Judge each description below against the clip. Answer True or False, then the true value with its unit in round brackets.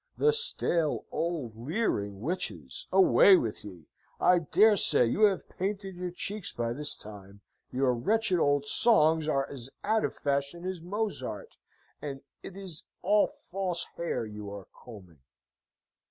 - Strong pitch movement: True (8.5 semitones)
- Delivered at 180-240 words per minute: False (145 wpm)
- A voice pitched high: False (160 Hz)